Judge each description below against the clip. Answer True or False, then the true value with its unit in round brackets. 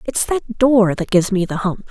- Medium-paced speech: False (250 wpm)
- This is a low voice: False (210 Hz)